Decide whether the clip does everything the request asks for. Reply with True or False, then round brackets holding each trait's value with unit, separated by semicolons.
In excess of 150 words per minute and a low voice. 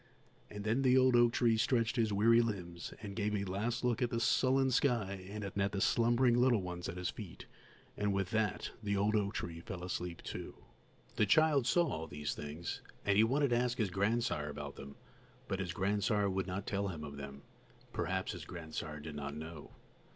True (200 wpm; 100 Hz)